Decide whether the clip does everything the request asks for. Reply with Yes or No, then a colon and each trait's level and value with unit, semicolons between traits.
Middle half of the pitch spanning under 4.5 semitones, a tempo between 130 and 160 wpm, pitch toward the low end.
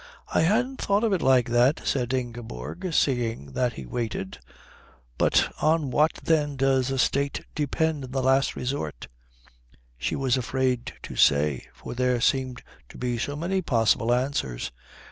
Yes: average, 3.4 semitones; average, 155 wpm; low, 130 Hz